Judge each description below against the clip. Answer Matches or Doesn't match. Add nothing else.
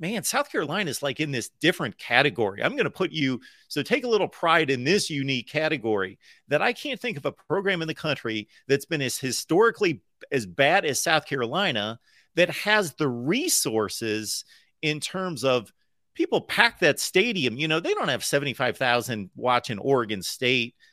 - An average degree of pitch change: Doesn't match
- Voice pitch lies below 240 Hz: Matches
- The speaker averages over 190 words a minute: Doesn't match